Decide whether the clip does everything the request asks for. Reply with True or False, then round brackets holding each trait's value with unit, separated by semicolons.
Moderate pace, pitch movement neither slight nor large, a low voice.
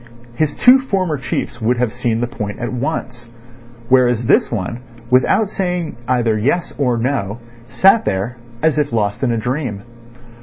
True (160 wpm; 4.6 semitones; 125 Hz)